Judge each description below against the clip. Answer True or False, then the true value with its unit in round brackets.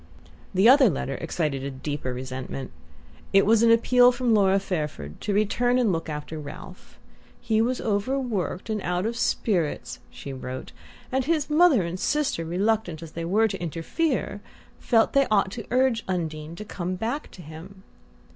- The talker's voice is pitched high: True (195 Hz)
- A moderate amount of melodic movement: False (6.3 semitones)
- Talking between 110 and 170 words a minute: True (165 wpm)